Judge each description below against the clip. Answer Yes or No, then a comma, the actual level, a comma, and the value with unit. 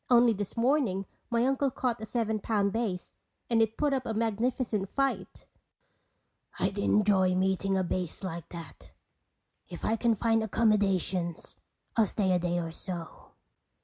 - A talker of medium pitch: No, high, 210 Hz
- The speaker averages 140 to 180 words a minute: Yes, average, 150 wpm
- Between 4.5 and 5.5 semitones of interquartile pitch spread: No, average, 3.8 semitones